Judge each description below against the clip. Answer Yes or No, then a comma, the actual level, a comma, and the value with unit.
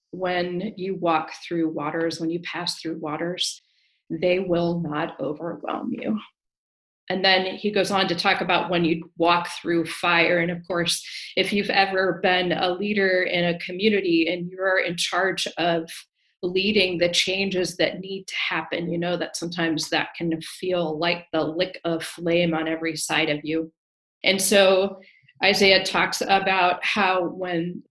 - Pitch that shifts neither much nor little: No, narrow, 2.1 semitones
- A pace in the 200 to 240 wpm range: No, average, 165 wpm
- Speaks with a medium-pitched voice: Yes, medium, 175 Hz